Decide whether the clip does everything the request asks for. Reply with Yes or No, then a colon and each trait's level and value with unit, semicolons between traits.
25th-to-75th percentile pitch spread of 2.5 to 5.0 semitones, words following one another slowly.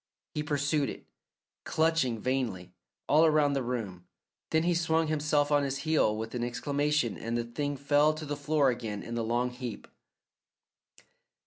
No: average, 4.2 semitones; average, 160 wpm